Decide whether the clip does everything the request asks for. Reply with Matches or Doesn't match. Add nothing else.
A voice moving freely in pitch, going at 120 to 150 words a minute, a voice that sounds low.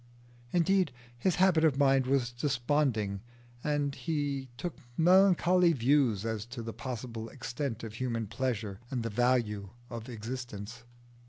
Doesn't match